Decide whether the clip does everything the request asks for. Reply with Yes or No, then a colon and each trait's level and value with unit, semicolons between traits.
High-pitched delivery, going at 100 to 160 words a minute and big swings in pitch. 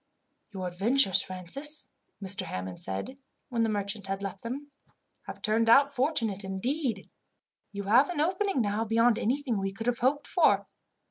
Yes: high, 225 Hz; average, 155 wpm; wide, 5.7 semitones